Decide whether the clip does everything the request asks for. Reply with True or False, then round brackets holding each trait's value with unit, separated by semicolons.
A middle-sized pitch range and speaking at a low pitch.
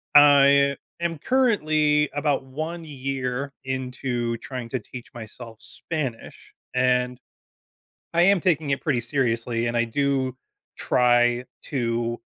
True (3.4 semitones; 130 Hz)